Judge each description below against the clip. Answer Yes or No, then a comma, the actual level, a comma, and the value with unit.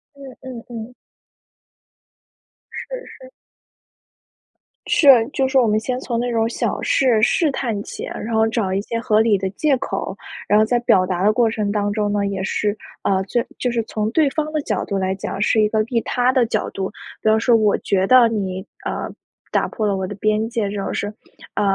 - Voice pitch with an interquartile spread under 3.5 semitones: Yes, average, 3.1 semitones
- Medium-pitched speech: No, high, 220 Hz